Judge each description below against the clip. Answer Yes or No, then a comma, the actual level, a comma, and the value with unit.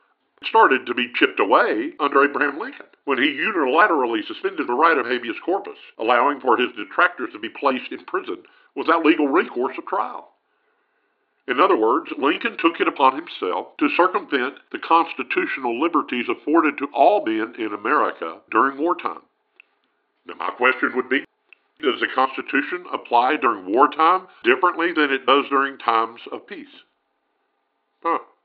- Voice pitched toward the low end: No, very high, 325 Hz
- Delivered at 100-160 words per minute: Yes, average, 150 wpm